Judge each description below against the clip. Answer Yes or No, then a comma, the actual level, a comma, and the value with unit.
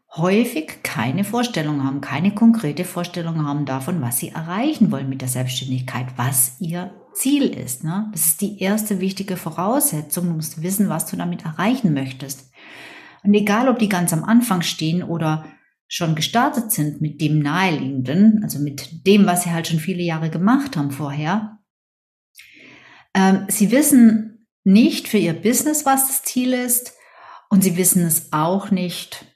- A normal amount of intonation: No, wide, 5.7 semitones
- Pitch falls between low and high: Yes, medium, 180 Hz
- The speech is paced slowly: No, average, 160 wpm